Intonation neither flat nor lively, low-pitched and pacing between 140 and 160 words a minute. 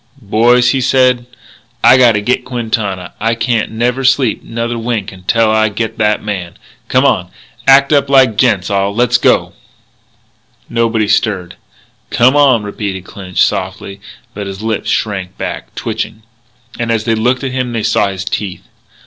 Yes: average, 3.2 semitones; low, 115 Hz; average, 155 wpm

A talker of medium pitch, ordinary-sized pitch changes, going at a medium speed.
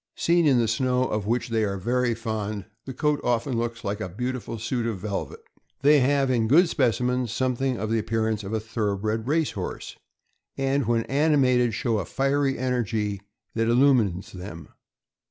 No: low, 115 Hz; average, 3.1 semitones; average, 180 wpm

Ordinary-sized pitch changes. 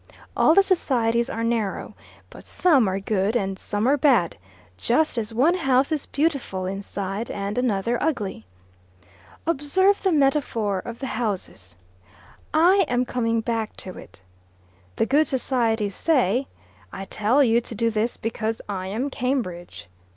Yes: average, 5.0 semitones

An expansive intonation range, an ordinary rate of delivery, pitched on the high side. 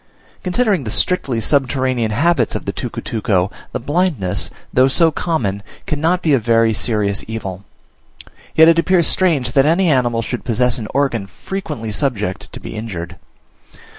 No: wide, 6.7 semitones; average, 150 wpm; low, 125 Hz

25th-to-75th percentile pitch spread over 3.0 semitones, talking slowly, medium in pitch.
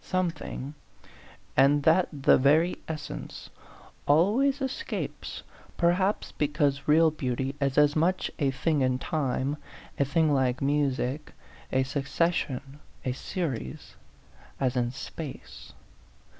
Yes: average, 3.6 semitones; slow, 115 wpm; medium, 145 Hz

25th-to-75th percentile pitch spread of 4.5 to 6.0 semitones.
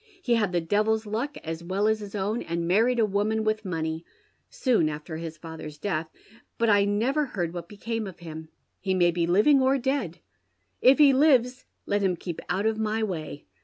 Yes: average, 5.0 semitones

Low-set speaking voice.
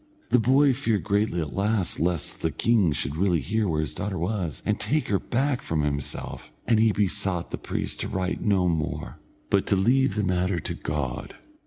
Yes: very low, 95 Hz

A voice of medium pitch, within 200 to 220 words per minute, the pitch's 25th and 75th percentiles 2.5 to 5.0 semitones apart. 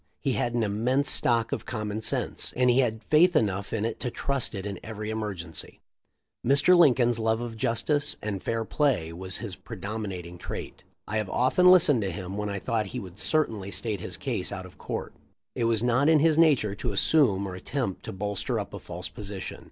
No: low, 110 Hz; fast, 205 wpm; average, 4.3 semitones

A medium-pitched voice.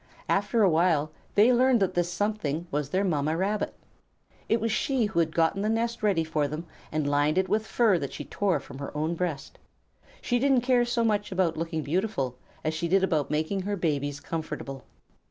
Yes: medium, 175 Hz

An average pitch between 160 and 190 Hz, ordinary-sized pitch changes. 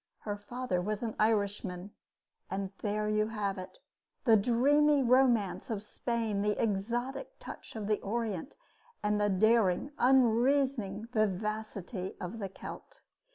No: high, 215 Hz; average, 3.0 semitones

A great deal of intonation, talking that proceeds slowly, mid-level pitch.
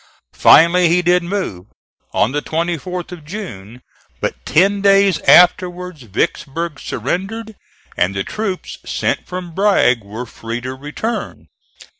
Yes: wide, 6.6 semitones; slow, 125 wpm; medium, 170 Hz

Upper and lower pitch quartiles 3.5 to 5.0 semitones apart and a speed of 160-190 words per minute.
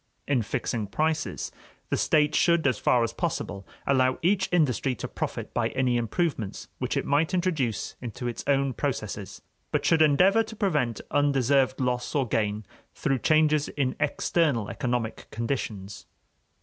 No: average, 4.7 semitones; average, 150 wpm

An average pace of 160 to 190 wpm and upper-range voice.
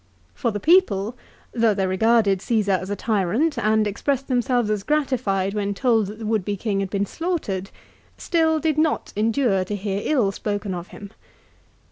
Yes: average, 175 wpm; high, 215 Hz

